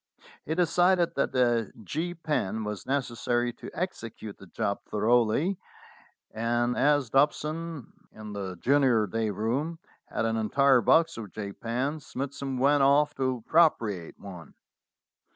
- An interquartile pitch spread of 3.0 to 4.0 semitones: No, average, 5.1 semitones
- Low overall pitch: Yes, low, 125 Hz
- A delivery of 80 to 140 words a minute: Yes, slow, 135 wpm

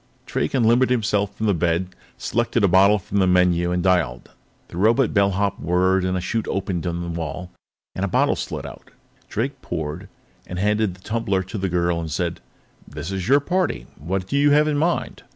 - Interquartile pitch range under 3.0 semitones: No, average, 3.9 semitones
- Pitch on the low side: Yes, very low, 95 Hz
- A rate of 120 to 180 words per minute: No, average, 190 wpm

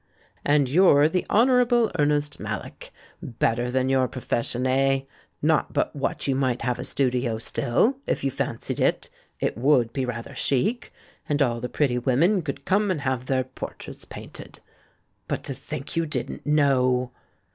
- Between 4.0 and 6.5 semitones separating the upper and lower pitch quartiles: No, average, 3.0 semitones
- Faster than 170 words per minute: No, average, 160 wpm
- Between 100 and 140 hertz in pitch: Yes, low, 135 Hz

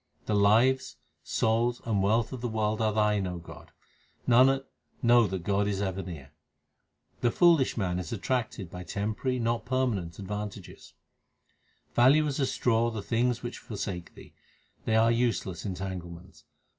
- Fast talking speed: No, average, 155 wpm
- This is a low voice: Yes, low, 110 Hz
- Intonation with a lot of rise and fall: No, average, 3.9 semitones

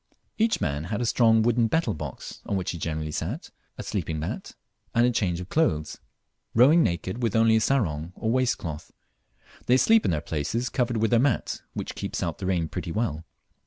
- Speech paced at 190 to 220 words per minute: Yes, average, 200 wpm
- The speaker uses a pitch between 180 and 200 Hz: No, low, 110 Hz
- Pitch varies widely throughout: Yes, wide, 6.7 semitones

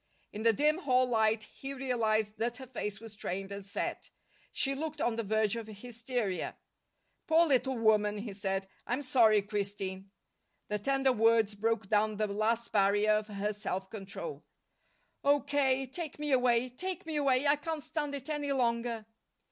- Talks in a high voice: Yes, high, 230 Hz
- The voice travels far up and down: No, average, 4.4 semitones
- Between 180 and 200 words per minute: No, average, 170 wpm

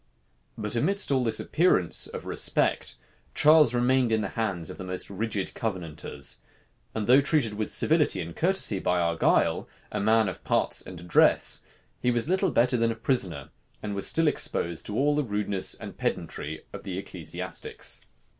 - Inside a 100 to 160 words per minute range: No, average, 170 wpm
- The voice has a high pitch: No, low, 110 Hz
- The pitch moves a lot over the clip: Yes, wide, 6.0 semitones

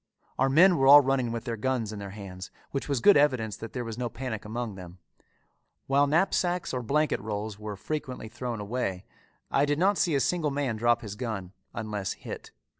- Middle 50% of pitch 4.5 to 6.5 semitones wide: Yes, average, 4.9 semitones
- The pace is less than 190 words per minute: No, average, 200 wpm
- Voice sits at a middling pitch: No, low, 120 Hz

